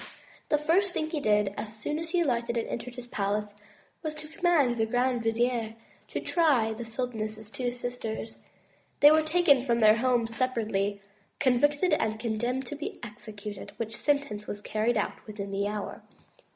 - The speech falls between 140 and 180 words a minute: Yes, average, 170 wpm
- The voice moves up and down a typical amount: Yes, average, 4.7 semitones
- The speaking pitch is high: Yes, high, 240 Hz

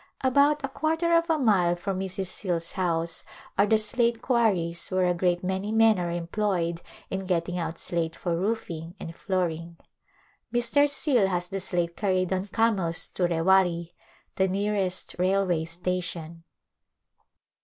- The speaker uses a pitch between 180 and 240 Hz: Yes, medium, 185 Hz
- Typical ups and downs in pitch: Yes, average, 3.7 semitones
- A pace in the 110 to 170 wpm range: Yes, average, 150 wpm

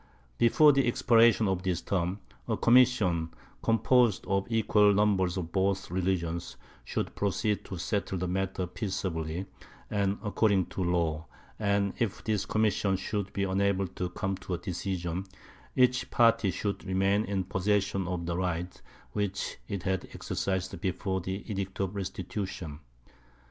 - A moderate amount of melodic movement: No, narrow, 2.2 semitones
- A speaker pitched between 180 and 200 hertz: No, very low, 95 Hz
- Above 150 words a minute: No, average, 145 wpm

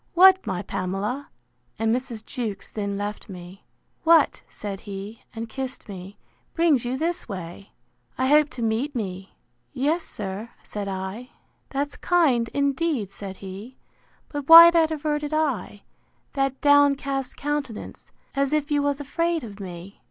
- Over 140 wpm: No, slow, 135 wpm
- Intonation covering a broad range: Yes, wide, 6.5 semitones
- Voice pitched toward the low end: No, very high, 255 Hz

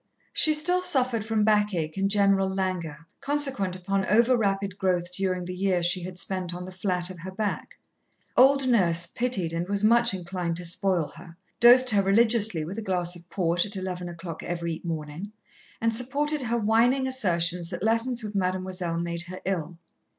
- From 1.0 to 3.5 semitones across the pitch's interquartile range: No, average, 4.1 semitones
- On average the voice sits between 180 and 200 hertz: Yes, high, 190 Hz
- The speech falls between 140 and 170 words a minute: No, average, 180 wpm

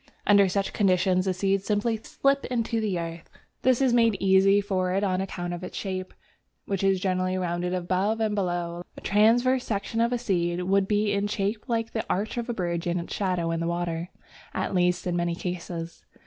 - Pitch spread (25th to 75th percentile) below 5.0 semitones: Yes, average, 3.1 semitones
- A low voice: No, high, 190 Hz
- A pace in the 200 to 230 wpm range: Yes, fast, 205 wpm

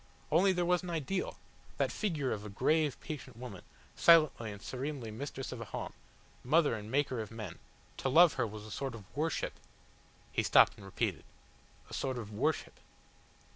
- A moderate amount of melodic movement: No, wide, 6.3 semitones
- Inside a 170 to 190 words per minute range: Yes, average, 180 wpm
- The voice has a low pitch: Yes, low, 130 Hz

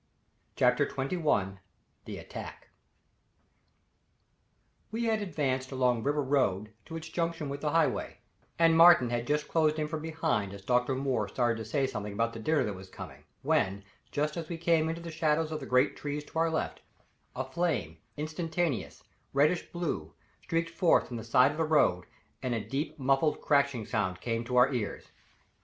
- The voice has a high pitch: No, medium, 140 Hz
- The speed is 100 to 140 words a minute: No, average, 175 wpm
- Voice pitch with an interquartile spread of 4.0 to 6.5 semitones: Yes, average, 5.2 semitones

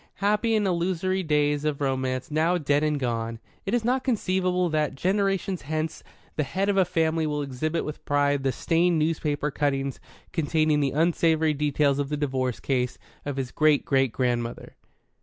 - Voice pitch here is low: No, medium, 150 Hz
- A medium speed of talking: Yes, average, 170 wpm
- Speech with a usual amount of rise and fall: Yes, average, 4.0 semitones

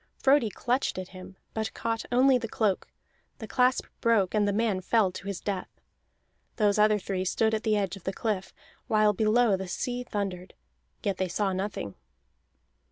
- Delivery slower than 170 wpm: No, average, 175 wpm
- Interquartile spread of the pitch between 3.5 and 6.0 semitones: No, average, 3.0 semitones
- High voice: Yes, high, 210 Hz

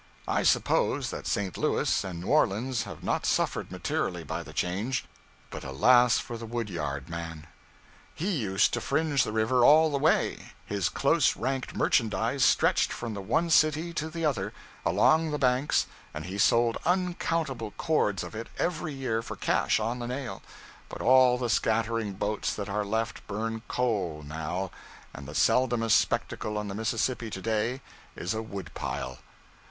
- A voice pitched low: Yes, low, 115 Hz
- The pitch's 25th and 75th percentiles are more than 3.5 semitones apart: Yes, average, 4.8 semitones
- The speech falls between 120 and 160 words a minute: No, average, 170 wpm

